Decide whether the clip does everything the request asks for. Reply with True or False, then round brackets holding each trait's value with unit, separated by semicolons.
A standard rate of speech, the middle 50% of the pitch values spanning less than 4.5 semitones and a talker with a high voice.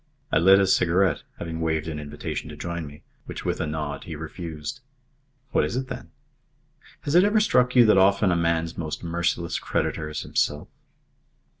False (180 wpm; 3.8 semitones; 85 Hz)